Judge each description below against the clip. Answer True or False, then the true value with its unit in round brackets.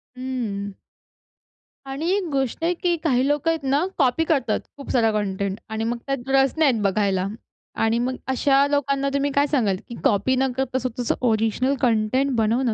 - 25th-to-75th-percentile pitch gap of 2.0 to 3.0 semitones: False (3.8 semitones)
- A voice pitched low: False (255 Hz)